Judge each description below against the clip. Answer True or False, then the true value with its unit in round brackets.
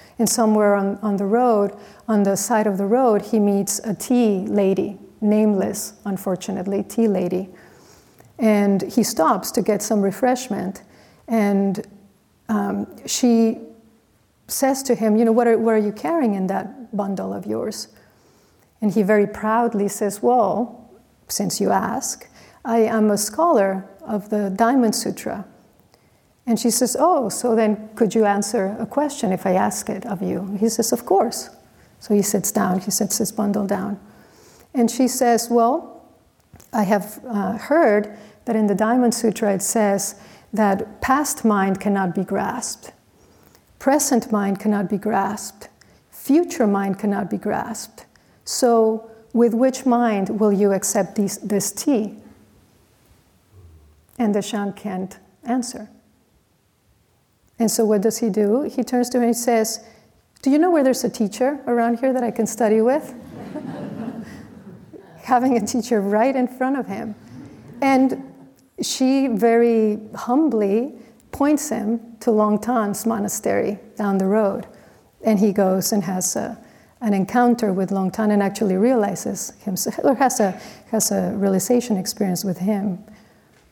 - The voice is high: True (215 Hz)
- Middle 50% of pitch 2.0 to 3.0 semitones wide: True (2.7 semitones)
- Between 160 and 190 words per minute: False (150 wpm)